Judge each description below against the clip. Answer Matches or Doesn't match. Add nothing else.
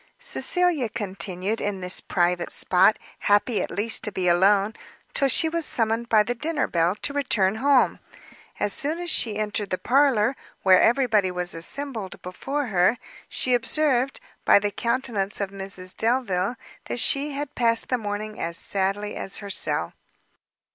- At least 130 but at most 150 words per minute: Doesn't match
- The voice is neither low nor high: Doesn't match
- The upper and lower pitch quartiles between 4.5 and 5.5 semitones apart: Matches